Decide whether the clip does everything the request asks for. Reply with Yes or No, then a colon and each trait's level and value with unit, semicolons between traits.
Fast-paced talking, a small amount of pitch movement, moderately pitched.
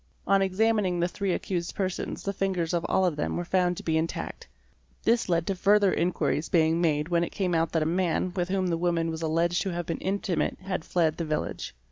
Yes: fast, 225 wpm; narrow, 2.3 semitones; medium, 175 Hz